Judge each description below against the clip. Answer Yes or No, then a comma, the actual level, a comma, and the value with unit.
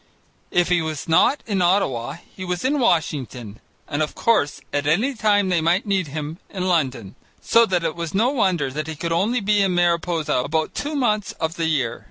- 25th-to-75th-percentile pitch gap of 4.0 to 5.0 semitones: Yes, average, 4.6 semitones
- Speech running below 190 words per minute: No, fast, 205 wpm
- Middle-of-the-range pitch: Yes, medium, 170 Hz